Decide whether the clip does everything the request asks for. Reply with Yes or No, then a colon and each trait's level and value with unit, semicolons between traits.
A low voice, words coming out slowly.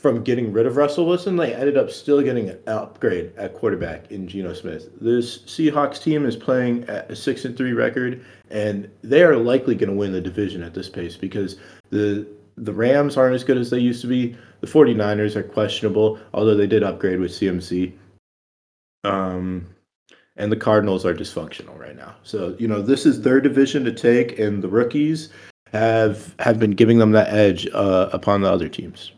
No: low, 110 Hz; average, 195 wpm